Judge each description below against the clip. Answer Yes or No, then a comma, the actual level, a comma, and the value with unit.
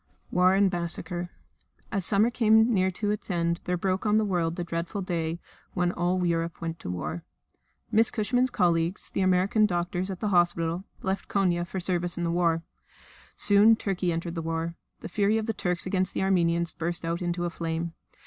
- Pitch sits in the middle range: Yes, medium, 180 Hz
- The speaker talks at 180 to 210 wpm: Yes, average, 190 wpm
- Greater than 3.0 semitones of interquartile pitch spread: No, narrow, 2.5 semitones